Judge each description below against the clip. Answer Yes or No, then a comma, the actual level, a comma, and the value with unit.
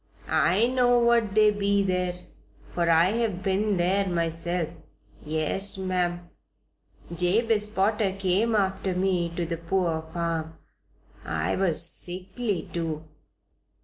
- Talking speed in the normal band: No, slow, 115 wpm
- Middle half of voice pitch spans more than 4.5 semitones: No, average, 3.1 semitones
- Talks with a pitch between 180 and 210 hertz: Yes, medium, 185 Hz